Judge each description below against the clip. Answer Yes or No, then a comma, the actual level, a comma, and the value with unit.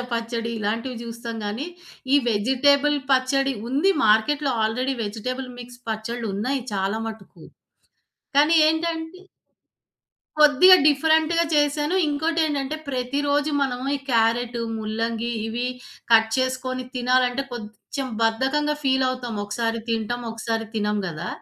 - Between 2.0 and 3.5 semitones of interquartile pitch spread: No, average, 4.0 semitones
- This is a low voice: No, very high, 250 Hz